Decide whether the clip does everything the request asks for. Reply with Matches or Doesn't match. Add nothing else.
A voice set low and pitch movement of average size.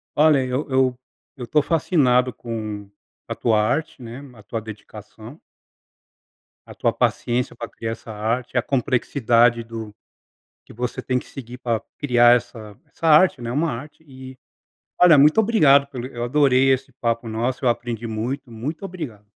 Matches